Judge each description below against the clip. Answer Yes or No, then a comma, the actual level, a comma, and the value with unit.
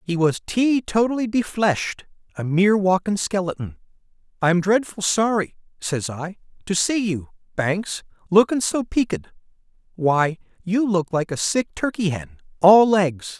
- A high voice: Yes, high, 195 Hz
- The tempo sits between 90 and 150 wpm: Yes, average, 140 wpm